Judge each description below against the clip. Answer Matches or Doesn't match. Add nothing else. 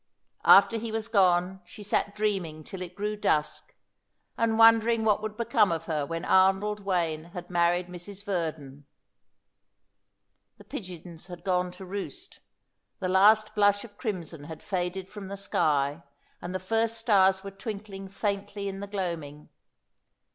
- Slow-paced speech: Doesn't match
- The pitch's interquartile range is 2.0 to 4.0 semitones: Matches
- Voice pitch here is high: Matches